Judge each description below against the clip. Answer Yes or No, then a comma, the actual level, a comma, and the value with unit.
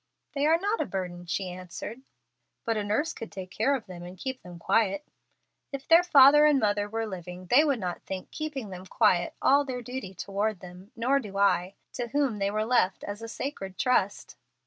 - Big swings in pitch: Yes, wide, 6.0 semitones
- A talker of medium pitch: No, high, 215 Hz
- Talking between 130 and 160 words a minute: No, fast, 205 wpm